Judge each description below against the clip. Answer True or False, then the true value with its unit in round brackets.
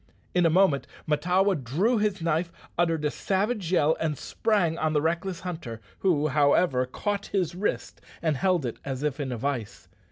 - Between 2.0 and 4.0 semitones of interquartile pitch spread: False (4.5 semitones)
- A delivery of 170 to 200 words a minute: True (180 wpm)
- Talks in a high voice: False (165 Hz)